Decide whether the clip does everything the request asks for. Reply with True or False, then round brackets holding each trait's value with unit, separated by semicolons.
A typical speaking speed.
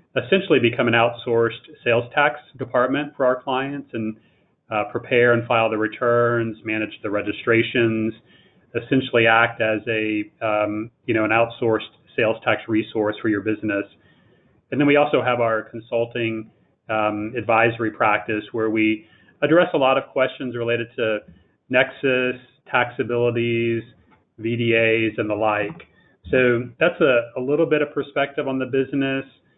True (145 wpm)